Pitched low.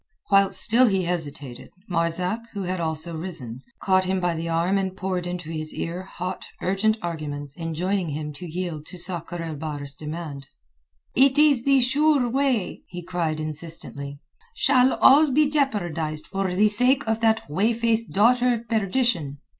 No: medium, 180 Hz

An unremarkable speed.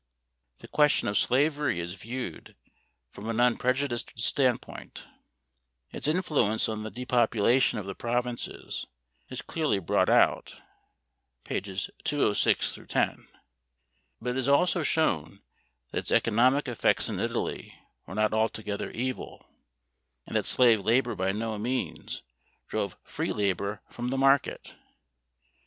No: slow, 125 wpm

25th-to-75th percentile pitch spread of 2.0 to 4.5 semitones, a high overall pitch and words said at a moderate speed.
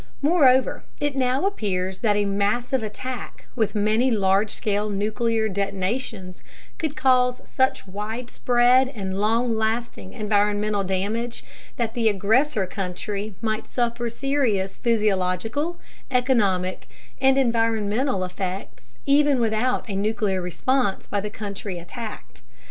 No: average, 3.9 semitones; high, 220 Hz; slow, 115 wpm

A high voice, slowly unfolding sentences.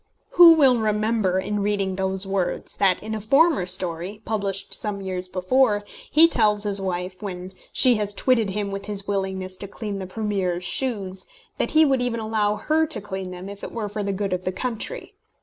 No: high, 205 Hz; average, 200 wpm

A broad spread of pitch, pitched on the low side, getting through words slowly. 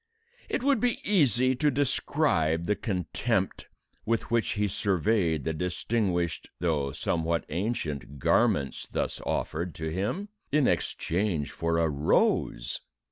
Yes: wide, 6.6 semitones; very low, 90 Hz; slow, 125 wpm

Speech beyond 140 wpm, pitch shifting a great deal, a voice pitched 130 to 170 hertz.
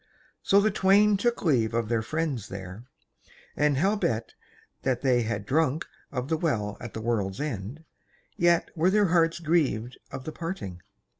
Yes: average, 160 wpm; wide, 7.0 semitones; medium, 140 Hz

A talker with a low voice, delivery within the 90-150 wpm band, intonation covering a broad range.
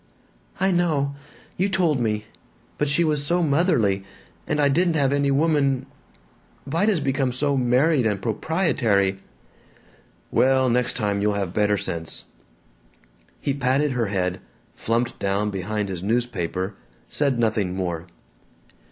Yes: low, 125 Hz; slow, 135 wpm; wide, 6.1 semitones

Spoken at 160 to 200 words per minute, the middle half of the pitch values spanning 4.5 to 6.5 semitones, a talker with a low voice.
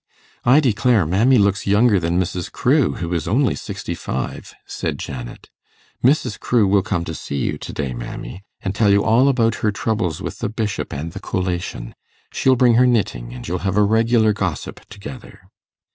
Yes: average, 185 wpm; average, 5.0 semitones; low, 100 Hz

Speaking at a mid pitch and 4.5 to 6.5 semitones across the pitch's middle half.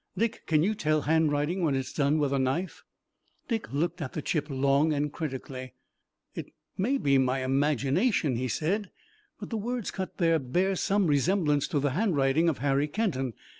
Yes: medium, 150 Hz; average, 5.0 semitones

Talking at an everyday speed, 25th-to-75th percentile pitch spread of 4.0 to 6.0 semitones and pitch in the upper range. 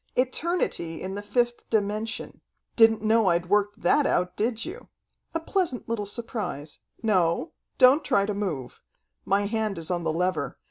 Yes: average, 155 wpm; average, 4.3 semitones; high, 210 Hz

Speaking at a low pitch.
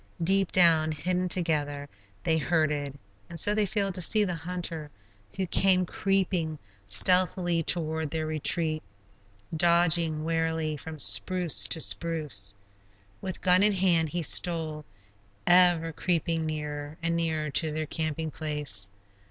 No: medium, 165 Hz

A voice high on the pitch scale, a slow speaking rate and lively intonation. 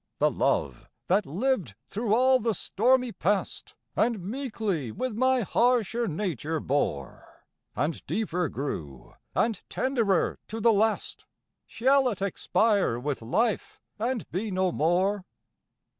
Yes: high, 205 Hz; slow, 125 wpm; wide, 5.9 semitones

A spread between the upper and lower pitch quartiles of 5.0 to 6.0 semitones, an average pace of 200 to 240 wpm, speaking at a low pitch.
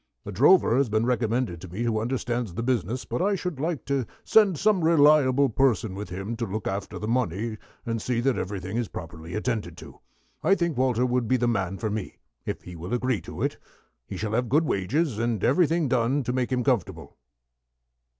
No: average, 4.3 semitones; fast, 205 wpm; low, 120 Hz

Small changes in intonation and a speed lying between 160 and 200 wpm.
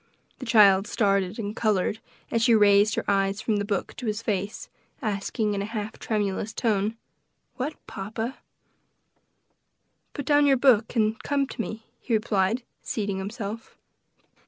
No: narrow, 2.3 semitones; average, 150 wpm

